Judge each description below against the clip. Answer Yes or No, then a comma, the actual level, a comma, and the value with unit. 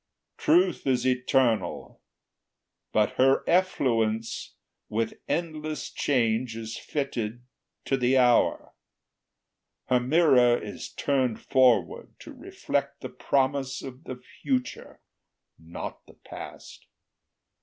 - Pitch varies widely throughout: No, average, 3.5 semitones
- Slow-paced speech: Yes, slow, 100 wpm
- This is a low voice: Yes, low, 130 Hz